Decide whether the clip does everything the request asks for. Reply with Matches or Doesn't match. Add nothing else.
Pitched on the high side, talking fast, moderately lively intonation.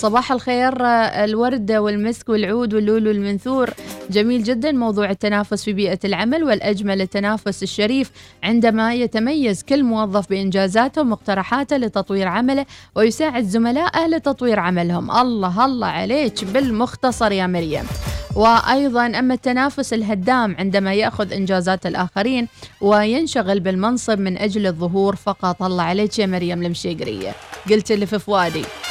Doesn't match